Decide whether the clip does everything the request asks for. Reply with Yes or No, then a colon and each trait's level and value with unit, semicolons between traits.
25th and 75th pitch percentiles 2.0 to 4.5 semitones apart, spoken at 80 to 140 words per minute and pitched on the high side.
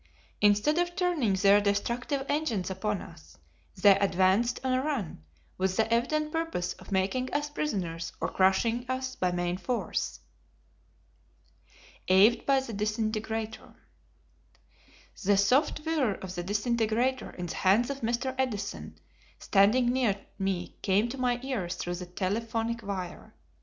No: average, 5.1 semitones; slow, 135 wpm; high, 220 Hz